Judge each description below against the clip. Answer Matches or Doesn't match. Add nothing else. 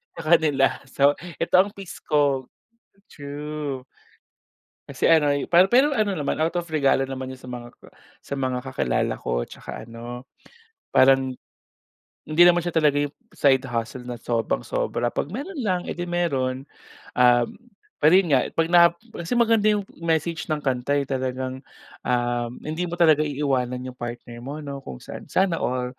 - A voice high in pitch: Doesn't match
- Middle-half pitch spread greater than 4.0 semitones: Matches